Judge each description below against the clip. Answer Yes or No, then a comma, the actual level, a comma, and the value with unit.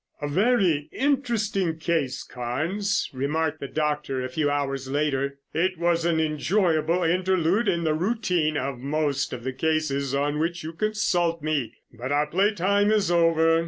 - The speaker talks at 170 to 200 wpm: No, average, 160 wpm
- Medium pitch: Yes, medium, 160 Hz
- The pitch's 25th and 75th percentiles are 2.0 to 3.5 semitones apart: No, average, 4.0 semitones